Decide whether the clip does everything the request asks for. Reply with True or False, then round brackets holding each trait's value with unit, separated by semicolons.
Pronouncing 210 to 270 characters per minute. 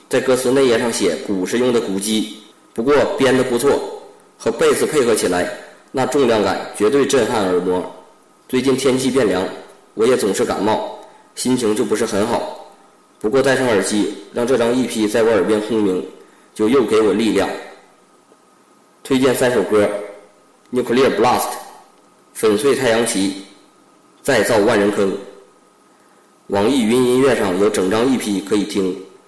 True (245 characters per minute)